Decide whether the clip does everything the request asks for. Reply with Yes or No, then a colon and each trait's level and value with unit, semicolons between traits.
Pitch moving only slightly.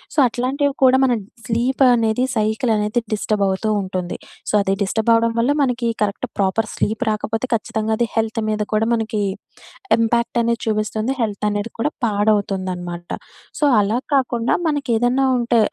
Yes: narrow, 2.3 semitones